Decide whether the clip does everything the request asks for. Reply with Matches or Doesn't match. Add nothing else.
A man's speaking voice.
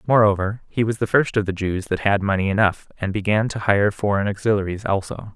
Matches